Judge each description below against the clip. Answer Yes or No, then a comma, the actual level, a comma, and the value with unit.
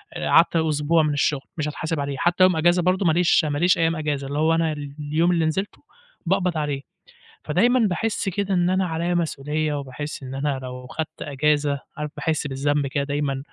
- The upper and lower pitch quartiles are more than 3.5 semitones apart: No, average, 3.1 semitones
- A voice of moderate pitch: Yes, medium, 155 Hz